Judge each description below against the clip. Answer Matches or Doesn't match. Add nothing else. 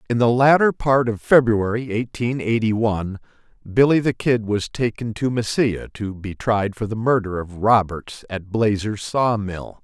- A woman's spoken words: Doesn't match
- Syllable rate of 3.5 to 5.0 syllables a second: Matches